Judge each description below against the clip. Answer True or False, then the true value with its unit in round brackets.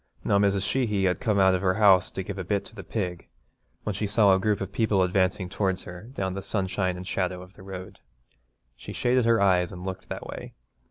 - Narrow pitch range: True (1.7 semitones)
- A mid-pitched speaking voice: False (95 Hz)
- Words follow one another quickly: True (230 wpm)